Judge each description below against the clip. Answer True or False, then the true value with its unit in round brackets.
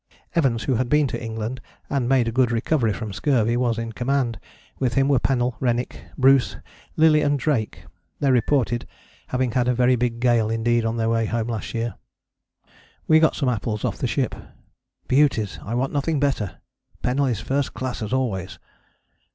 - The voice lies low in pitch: True (125 Hz)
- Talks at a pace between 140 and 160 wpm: False (180 wpm)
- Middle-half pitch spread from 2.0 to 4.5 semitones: True (2.8 semitones)